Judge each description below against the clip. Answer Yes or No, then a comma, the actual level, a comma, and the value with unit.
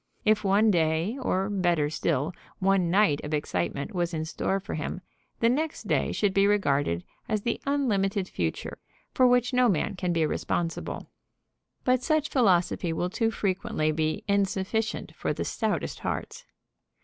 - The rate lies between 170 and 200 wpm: No, average, 155 wpm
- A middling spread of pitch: Yes, average, 5.0 semitones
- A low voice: No, high, 190 Hz